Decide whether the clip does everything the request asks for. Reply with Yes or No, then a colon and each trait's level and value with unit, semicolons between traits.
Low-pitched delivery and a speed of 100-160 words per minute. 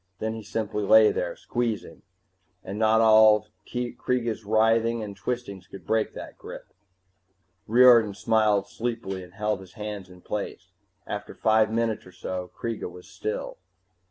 Yes: low, 110 Hz; average, 145 wpm